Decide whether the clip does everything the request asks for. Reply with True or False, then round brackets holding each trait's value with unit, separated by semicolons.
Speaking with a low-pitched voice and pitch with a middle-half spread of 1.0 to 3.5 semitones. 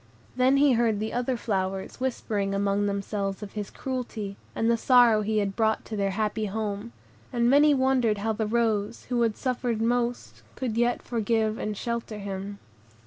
False (220 Hz; 2.8 semitones)